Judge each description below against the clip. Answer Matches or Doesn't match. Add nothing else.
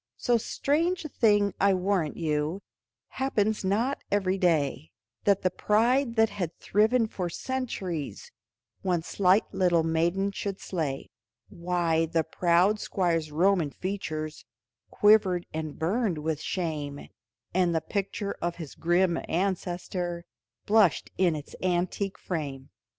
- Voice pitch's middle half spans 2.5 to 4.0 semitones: Matches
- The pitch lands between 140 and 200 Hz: Matches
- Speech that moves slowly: Matches